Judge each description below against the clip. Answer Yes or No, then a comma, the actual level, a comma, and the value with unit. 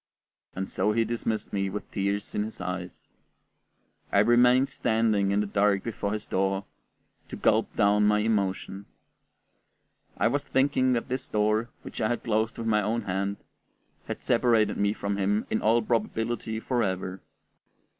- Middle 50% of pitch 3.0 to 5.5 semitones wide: No, narrow, 2.4 semitones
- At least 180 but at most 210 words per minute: No, average, 155 wpm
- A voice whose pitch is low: Yes, low, 105 Hz